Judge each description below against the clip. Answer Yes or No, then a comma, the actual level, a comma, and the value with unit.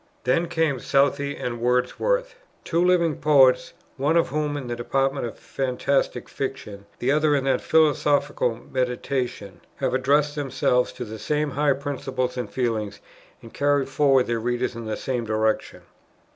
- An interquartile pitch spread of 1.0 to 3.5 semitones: Yes, average, 2.9 semitones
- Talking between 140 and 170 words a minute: Yes, average, 160 wpm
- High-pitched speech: No, low, 135 Hz